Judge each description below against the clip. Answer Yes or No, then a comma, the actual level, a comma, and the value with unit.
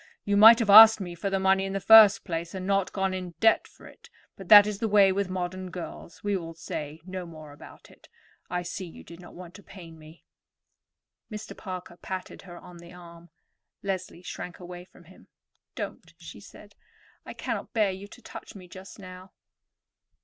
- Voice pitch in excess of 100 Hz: Yes, medium, 185 Hz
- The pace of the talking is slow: No, average, 200 wpm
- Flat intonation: Yes, narrow, 2.2 semitones